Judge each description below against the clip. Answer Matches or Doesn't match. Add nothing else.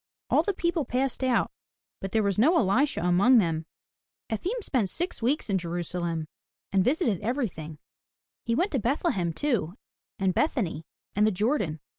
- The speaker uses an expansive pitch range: Matches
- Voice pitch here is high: Matches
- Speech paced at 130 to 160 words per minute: Matches